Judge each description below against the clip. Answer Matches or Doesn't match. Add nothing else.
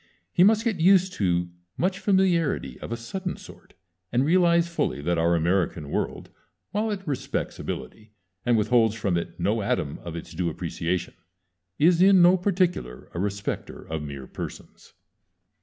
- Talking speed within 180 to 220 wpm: Doesn't match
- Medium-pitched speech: Doesn't match